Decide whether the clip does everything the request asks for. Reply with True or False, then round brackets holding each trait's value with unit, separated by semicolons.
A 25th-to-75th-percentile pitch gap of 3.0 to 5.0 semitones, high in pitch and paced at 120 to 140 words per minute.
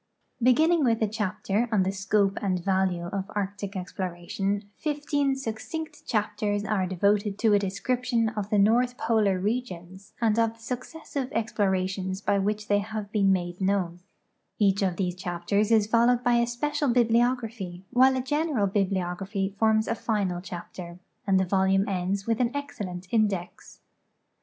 False (3.4 semitones; 205 Hz; 155 wpm)